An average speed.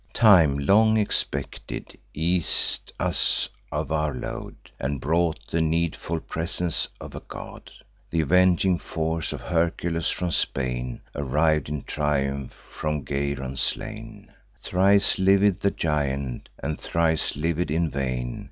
No: slow, 125 wpm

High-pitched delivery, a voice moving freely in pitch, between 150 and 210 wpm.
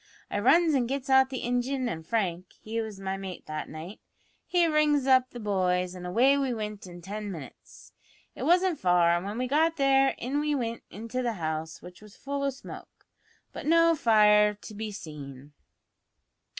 Yes: high, 225 Hz; wide, 6.7 semitones; average, 190 wpm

